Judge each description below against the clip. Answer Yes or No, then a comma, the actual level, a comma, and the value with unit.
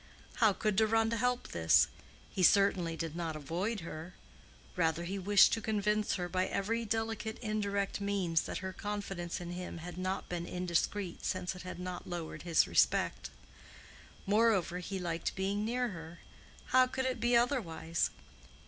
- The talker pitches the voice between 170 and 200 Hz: Yes, high, 190 Hz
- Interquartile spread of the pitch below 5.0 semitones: Yes, average, 3.7 semitones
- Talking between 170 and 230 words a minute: No, average, 155 wpm